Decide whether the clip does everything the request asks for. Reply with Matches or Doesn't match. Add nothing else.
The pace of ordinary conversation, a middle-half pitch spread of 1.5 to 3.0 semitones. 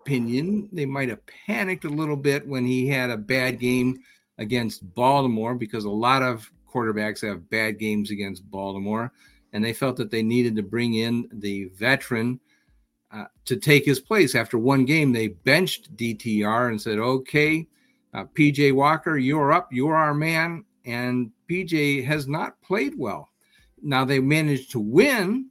Doesn't match